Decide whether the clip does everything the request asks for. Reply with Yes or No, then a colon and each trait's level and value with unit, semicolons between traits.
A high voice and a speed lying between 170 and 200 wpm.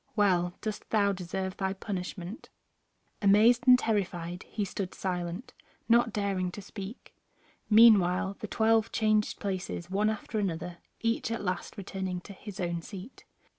No: high, 200 Hz; average, 140 wpm